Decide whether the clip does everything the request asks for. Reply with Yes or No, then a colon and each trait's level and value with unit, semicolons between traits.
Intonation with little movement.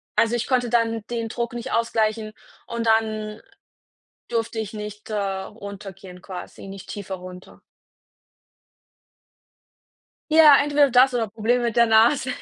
Yes: narrow, 2.3 semitones